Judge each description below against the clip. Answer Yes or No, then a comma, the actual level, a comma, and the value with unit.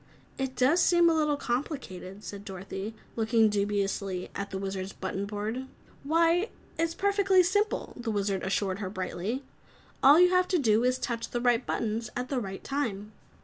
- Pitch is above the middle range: Yes, high, 230 Hz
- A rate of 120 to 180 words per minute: Yes, average, 170 wpm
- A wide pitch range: Yes, wide, 6.7 semitones